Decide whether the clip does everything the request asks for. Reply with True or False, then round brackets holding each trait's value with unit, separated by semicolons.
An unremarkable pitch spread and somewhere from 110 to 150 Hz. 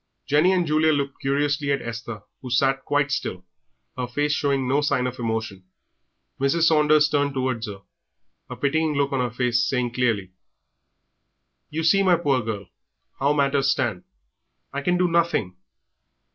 True (3.4 semitones; 140 Hz)